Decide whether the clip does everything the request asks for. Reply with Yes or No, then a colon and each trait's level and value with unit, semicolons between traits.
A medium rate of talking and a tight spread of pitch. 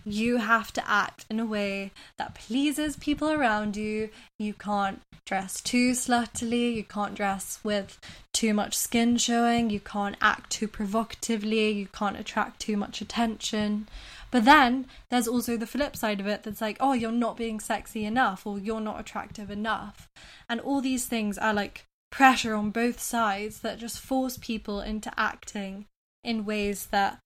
Yes: average, 170 wpm; narrow, 2.3 semitones